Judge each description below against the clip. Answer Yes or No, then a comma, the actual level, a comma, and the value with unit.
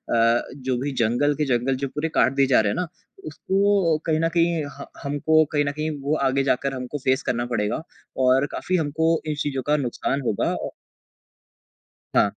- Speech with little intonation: No, average, 3.2 semitones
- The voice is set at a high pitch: No, medium, 140 Hz